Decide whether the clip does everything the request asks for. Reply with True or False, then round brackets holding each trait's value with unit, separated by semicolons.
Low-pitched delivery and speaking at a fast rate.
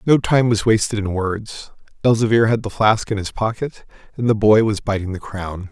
True (105 Hz; 210 wpm)